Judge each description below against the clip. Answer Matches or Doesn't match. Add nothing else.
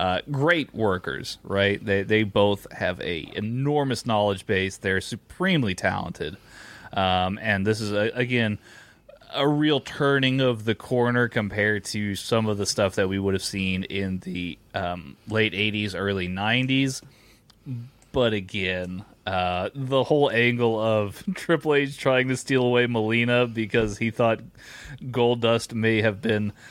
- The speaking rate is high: Doesn't match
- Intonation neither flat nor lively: Matches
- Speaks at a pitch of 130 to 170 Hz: Doesn't match